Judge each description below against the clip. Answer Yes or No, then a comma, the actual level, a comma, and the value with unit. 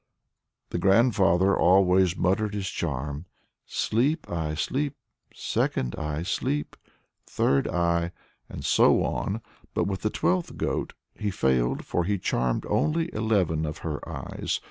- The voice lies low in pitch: Yes, very low, 90 Hz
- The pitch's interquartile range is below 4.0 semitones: No, average, 4.9 semitones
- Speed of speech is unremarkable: No, slow, 130 wpm